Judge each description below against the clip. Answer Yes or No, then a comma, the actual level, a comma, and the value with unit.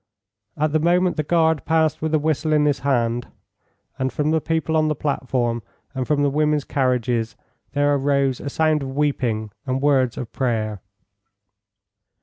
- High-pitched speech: No, medium, 145 Hz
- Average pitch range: Yes, average, 3.2 semitones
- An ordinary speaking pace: Yes, average, 165 wpm